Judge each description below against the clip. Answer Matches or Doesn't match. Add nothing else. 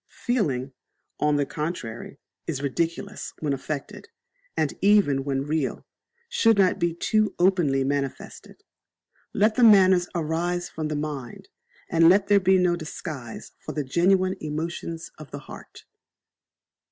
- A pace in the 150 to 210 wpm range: Doesn't match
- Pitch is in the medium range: Matches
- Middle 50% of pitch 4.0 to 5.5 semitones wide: Matches